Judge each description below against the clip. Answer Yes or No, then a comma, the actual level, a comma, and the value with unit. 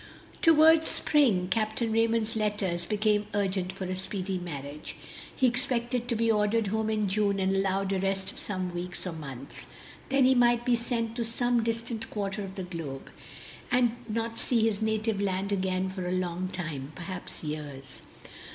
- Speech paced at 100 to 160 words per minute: No, average, 170 wpm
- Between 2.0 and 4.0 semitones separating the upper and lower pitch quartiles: Yes, average, 3.7 semitones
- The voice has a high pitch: Yes, high, 205 Hz